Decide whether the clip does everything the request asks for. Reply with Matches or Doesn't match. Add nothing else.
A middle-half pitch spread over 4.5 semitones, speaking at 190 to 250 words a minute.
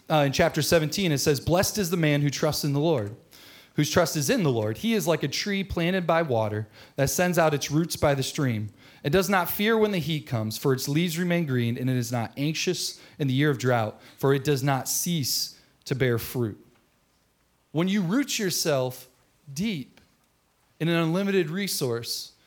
Matches